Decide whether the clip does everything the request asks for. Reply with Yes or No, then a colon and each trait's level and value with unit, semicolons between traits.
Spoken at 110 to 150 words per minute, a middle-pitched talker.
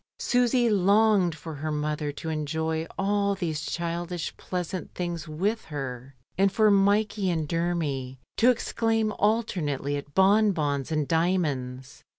Yes: slow, 135 wpm; medium, 170 Hz